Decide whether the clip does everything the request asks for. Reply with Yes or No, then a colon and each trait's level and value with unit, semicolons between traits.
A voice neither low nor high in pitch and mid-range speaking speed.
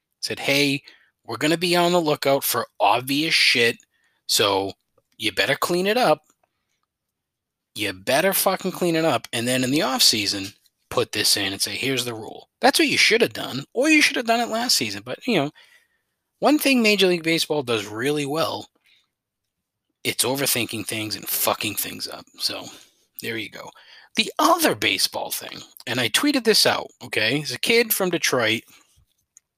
Yes: medium, 150 Hz; average, 180 wpm